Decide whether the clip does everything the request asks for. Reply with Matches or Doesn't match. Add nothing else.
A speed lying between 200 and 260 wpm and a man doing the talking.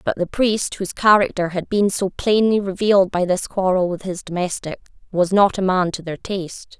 Doesn't match